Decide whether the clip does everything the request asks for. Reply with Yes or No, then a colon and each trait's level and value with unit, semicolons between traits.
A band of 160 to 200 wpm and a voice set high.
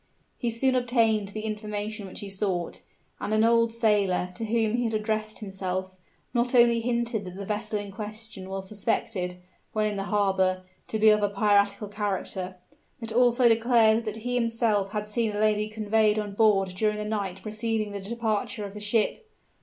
Yes: average, 180 wpm; high, 215 Hz